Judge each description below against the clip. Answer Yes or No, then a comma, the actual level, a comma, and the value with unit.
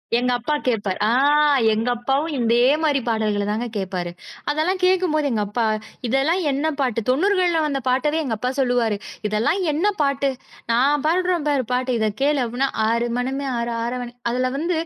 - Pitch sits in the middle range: No, very high, 255 Hz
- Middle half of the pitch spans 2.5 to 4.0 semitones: No, average, 4.6 semitones